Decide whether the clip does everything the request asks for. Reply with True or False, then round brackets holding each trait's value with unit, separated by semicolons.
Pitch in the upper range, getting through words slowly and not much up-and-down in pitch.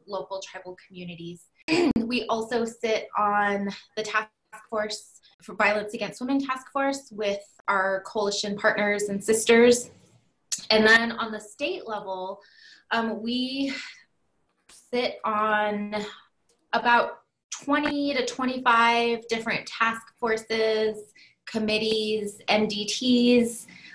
True (220 Hz; 105 wpm; 2.3 semitones)